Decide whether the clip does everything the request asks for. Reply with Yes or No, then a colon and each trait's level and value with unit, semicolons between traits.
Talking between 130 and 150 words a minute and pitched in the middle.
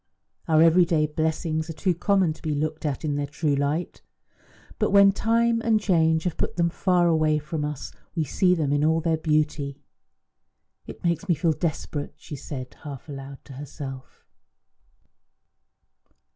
No: average, 160 wpm; medium, 155 Hz